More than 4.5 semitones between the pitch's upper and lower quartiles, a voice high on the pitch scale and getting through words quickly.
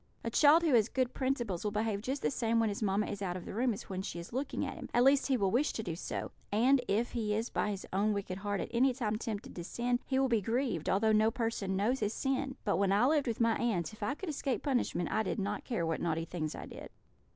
No: average, 4.2 semitones; high, 225 Hz; fast, 275 wpm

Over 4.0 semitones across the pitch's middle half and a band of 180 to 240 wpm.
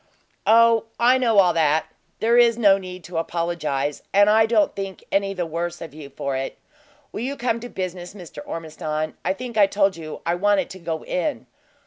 Yes: average, 4.9 semitones; average, 195 wpm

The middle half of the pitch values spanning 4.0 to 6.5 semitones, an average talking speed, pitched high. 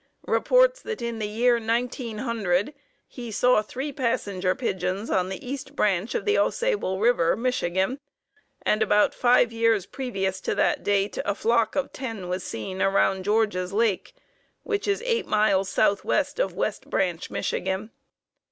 Yes: average, 4.7 semitones; average, 150 wpm; high, 220 Hz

